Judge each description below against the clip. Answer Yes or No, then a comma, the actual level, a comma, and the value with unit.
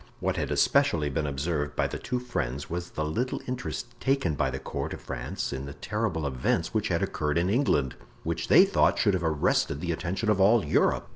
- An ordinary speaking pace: No, fast, 210 wpm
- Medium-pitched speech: No, very low, 80 Hz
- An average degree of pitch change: No, wide, 6.9 semitones